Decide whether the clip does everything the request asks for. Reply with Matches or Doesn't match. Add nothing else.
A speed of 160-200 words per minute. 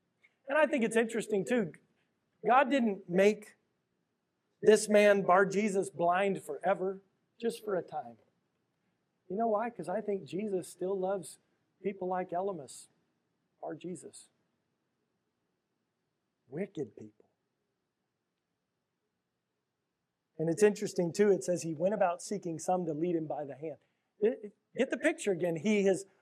Doesn't match